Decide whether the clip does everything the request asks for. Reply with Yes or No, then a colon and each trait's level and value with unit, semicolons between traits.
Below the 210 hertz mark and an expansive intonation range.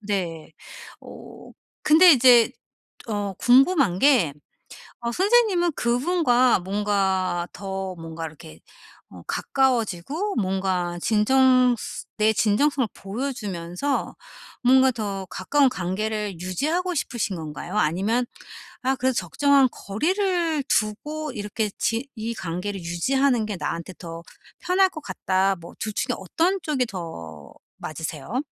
No: high, 215 Hz; wide, 6.5 semitones